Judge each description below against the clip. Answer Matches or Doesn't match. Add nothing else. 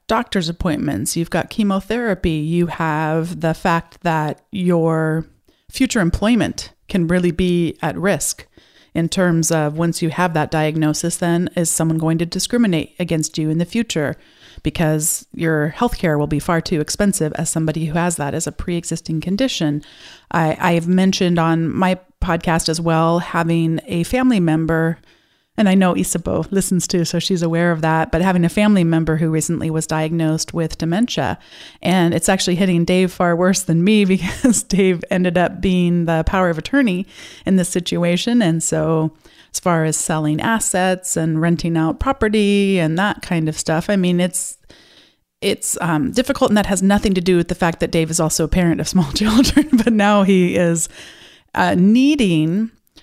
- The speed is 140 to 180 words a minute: Matches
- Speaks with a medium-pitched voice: Matches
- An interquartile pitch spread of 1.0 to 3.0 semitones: Matches